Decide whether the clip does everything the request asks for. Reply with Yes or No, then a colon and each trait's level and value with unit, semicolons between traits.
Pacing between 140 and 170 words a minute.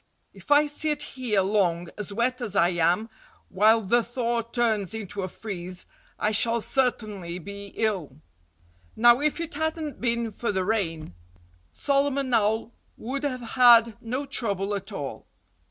Yes: average, 150 wpm